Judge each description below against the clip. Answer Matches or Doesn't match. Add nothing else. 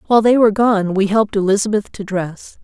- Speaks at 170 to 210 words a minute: Matches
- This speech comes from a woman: Matches